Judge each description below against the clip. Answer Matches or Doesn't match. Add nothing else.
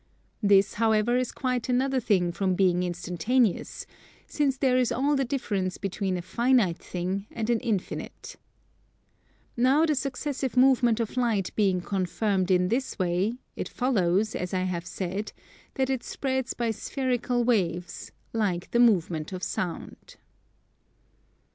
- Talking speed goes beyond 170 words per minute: Doesn't match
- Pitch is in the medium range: Doesn't match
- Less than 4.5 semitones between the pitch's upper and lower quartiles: Doesn't match